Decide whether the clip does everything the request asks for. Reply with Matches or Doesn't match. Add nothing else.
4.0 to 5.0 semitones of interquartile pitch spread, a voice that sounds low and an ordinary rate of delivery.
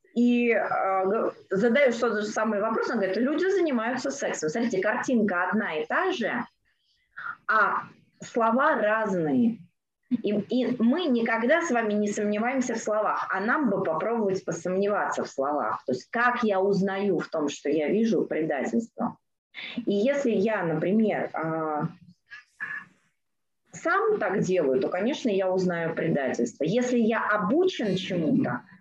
Doesn't match